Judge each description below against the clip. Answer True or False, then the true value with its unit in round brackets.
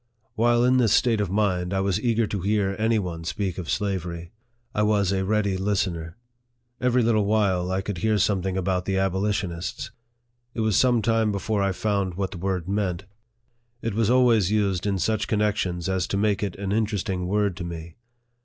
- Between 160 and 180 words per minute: False (190 wpm)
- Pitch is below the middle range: True (100 Hz)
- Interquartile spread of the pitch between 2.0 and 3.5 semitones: True (2.7 semitones)